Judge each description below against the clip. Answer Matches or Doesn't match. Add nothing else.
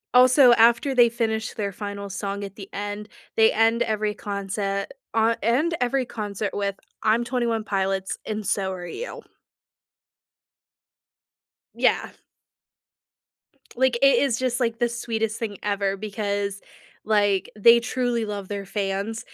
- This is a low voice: Doesn't match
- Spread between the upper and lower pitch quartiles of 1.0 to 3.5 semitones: Matches